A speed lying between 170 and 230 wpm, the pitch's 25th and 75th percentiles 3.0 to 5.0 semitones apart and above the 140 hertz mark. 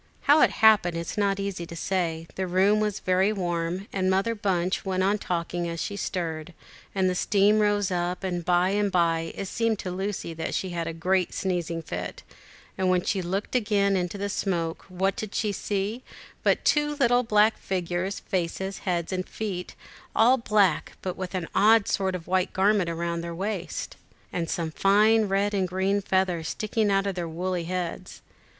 No: average, 190 wpm; narrow, 2.6 semitones; high, 190 Hz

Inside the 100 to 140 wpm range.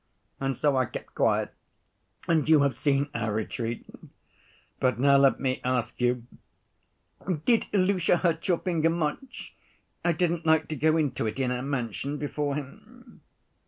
No: average, 155 wpm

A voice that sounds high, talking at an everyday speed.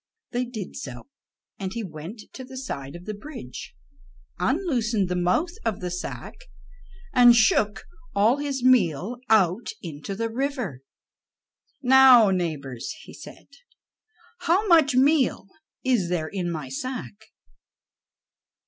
No: high, 220 Hz; slow, 125 wpm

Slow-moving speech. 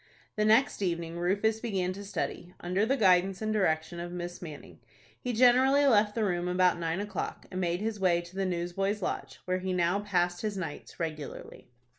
No: average, 190 wpm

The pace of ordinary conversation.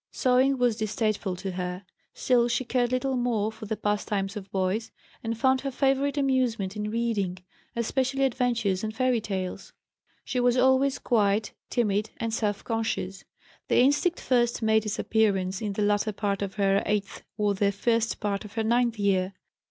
Yes: average, 170 wpm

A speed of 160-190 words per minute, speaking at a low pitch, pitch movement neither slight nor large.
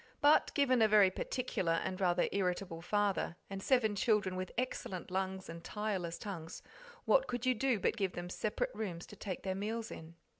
No: average, 185 wpm; high, 195 Hz; average, 3.7 semitones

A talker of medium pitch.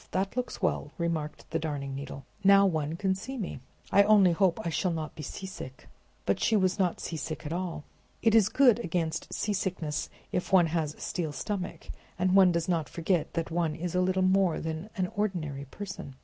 Yes: medium, 175 Hz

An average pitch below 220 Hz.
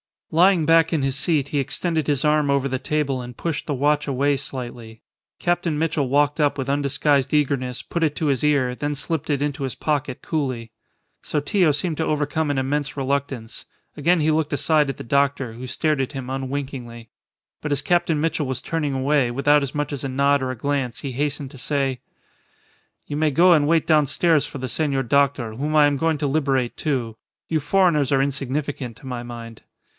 Yes: medium, 140 Hz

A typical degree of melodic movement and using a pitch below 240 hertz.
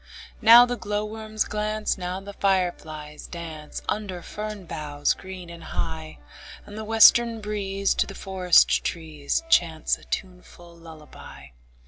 Yes: average, 4.5 semitones; high, 190 Hz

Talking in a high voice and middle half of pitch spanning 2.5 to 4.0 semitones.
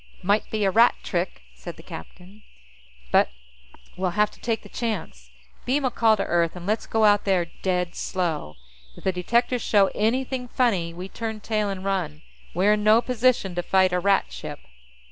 Yes: high, 195 Hz; average, 3.7 semitones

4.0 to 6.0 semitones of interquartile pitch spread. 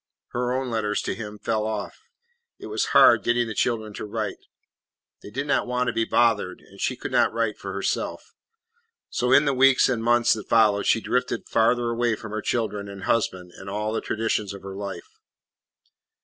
No: narrow, 2.5 semitones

